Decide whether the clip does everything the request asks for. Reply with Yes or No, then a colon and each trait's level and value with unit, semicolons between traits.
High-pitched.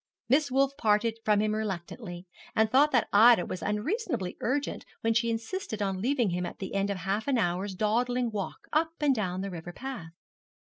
Yes: high, 220 Hz